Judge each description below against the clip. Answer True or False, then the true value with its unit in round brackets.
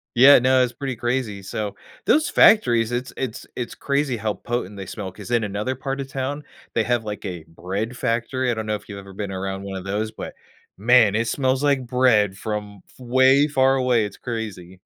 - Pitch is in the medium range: False (115 Hz)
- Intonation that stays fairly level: False (4.1 semitones)